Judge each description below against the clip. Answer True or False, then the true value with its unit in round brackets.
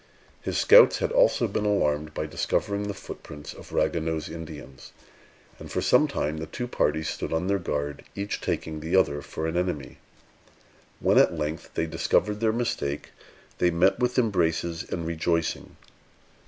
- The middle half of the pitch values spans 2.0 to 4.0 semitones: False (4.6 semitones)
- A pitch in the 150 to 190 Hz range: False (85 Hz)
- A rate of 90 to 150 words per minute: False (160 wpm)